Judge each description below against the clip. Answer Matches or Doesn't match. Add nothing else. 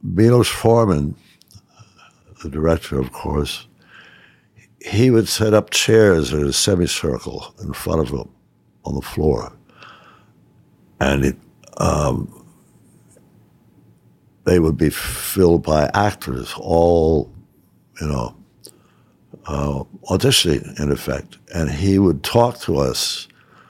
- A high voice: Doesn't match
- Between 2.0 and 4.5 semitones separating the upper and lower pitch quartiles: Doesn't match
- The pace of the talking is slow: Matches